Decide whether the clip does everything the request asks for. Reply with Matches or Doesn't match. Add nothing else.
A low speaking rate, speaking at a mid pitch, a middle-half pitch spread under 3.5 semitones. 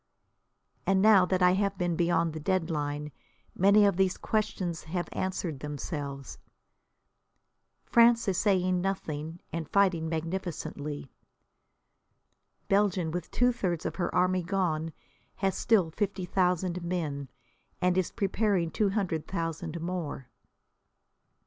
Matches